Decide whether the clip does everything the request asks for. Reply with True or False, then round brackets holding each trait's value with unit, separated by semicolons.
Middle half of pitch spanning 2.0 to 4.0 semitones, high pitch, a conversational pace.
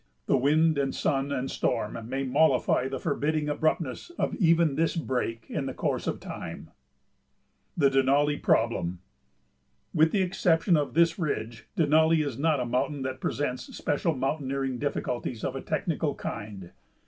False (3.6 semitones; 140 Hz; 155 wpm)